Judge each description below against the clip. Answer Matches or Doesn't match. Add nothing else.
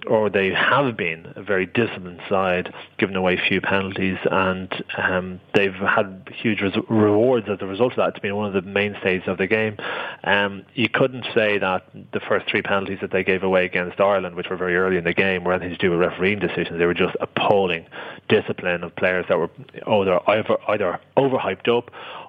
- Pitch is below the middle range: Matches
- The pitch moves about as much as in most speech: Doesn't match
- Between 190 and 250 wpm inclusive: Matches